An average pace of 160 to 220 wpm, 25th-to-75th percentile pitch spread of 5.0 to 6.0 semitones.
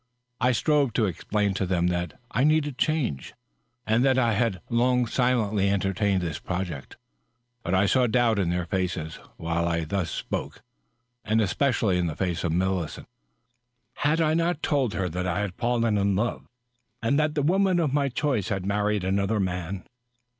Yes: average, 180 wpm; wide, 5.5 semitones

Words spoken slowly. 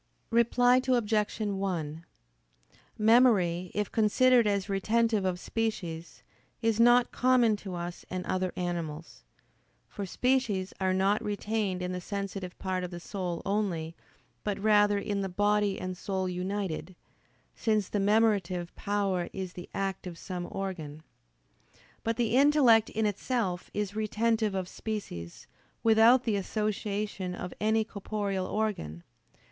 Yes: slow, 130 wpm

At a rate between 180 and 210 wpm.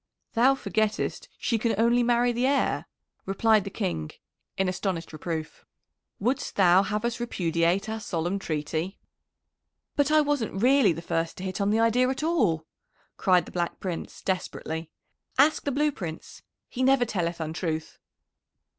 No: average, 155 wpm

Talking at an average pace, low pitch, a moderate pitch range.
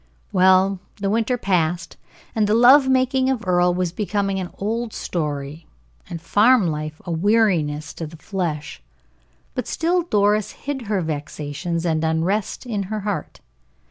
No: average, 145 wpm; high, 190 Hz; average, 5.0 semitones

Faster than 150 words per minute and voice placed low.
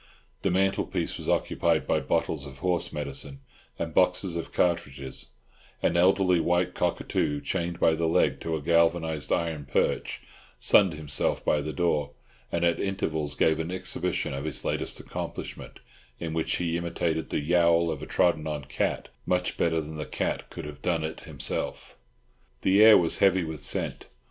Yes: average, 170 wpm; very low, 80 Hz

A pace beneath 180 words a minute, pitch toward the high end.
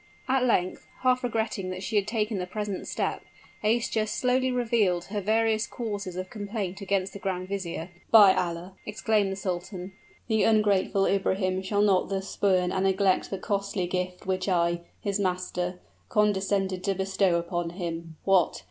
Yes: average, 160 wpm; high, 195 Hz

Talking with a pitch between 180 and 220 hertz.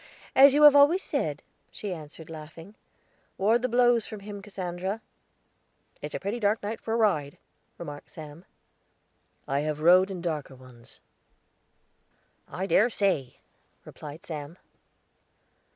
Yes: medium, 185 Hz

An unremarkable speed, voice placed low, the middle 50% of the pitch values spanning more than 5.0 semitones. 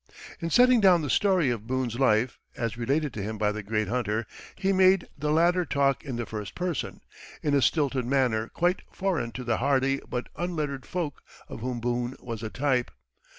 Yes: average, 195 wpm; low, 130 Hz; wide, 5.6 semitones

